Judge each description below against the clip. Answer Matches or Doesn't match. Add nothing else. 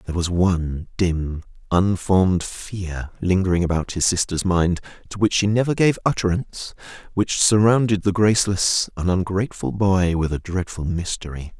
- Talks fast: Doesn't match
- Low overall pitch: Matches